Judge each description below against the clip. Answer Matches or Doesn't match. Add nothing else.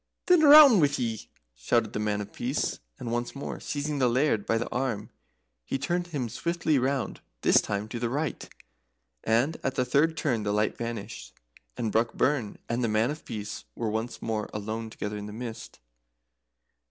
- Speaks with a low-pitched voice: Matches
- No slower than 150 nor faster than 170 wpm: Doesn't match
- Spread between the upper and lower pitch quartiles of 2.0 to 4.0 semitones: Doesn't match